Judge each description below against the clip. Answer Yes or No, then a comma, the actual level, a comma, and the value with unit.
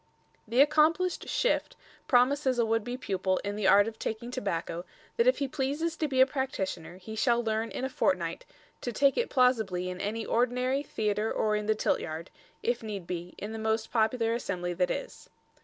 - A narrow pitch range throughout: No, average, 4.4 semitones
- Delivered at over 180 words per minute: Yes, average, 190 wpm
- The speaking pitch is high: Yes, high, 225 Hz